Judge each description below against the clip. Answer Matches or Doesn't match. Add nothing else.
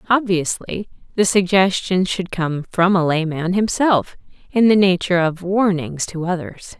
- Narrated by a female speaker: Matches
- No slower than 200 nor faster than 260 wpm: Doesn't match